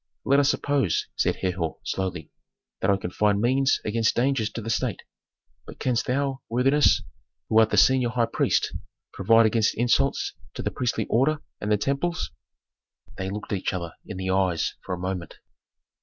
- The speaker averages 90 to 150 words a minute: No, average, 170 wpm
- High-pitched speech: No, low, 115 Hz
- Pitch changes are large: Yes, wide, 5.7 semitones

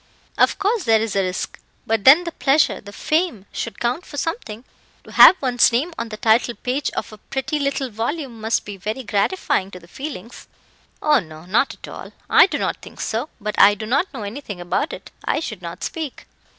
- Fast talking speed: Yes, fast, 210 wpm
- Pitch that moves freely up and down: Yes, wide, 5.7 semitones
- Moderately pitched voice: No, high, 235 Hz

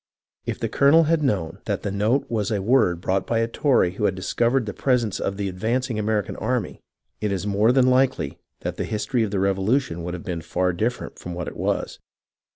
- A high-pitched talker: No, low, 105 Hz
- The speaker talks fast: Yes, fast, 225 wpm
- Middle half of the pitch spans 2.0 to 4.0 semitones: No, average, 4.7 semitones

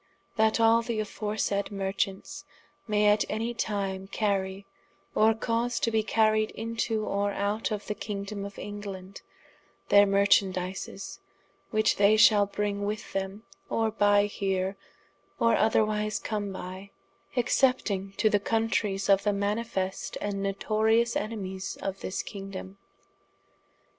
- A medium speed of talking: No, slow, 130 wpm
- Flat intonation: Yes, narrow, 1.8 semitones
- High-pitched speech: Yes, high, 205 Hz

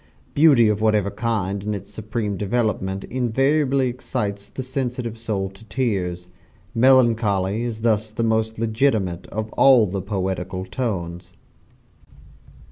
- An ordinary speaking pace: No, slow, 125 wpm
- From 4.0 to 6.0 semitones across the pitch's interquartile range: No, average, 3.6 semitones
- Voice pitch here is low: Yes, low, 110 Hz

